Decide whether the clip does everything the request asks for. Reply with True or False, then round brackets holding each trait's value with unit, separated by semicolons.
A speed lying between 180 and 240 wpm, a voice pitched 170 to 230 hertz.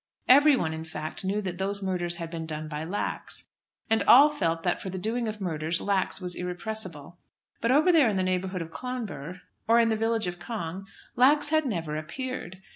True (200 wpm; 190 Hz)